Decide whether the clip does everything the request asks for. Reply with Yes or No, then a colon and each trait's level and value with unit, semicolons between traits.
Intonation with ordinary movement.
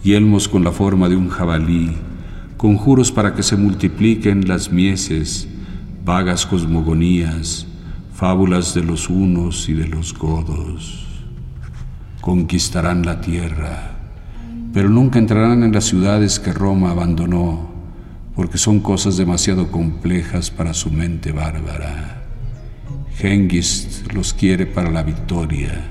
Yes: average, 3.0 semitones